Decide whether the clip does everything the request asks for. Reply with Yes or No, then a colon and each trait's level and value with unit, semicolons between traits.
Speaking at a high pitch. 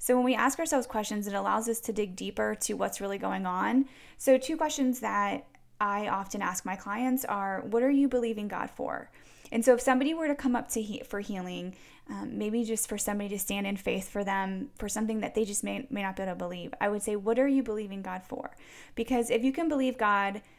Yes: high, 220 Hz